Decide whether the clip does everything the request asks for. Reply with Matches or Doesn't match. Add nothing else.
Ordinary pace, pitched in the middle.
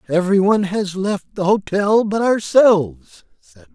Doesn't match